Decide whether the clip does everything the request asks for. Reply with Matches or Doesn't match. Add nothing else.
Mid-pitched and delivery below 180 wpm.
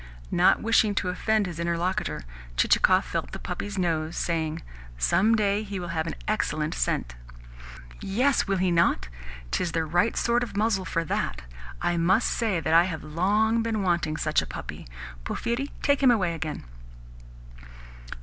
Matches